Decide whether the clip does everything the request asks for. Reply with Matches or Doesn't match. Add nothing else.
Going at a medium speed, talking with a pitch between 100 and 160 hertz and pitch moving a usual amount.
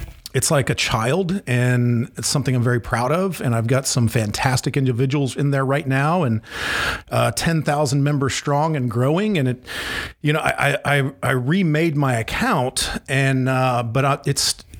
Matches